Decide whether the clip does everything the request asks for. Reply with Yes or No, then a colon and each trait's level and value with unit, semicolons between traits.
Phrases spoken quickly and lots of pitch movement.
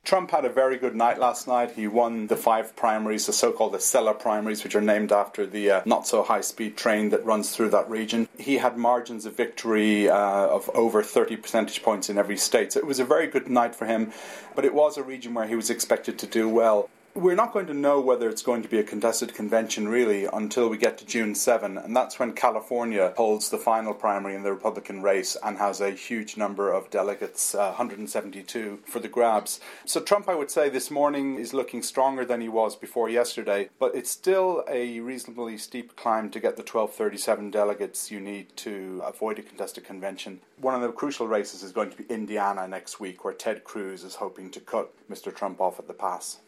No: fast, 225 wpm; average, 2.7 semitones